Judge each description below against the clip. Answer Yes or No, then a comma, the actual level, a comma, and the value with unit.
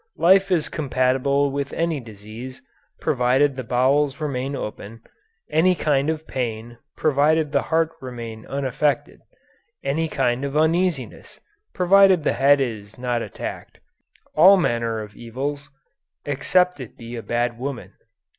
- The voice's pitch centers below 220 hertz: Yes, low, 135 Hz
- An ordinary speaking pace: No, slow, 130 wpm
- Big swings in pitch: No, average, 4.3 semitones